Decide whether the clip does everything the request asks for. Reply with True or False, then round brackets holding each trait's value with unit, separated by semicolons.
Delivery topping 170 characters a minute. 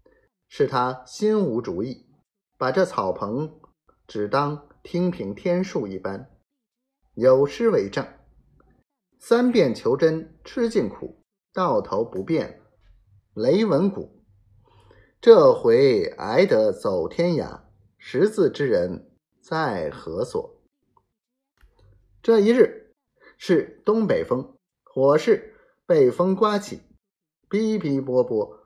False (140 characters per minute)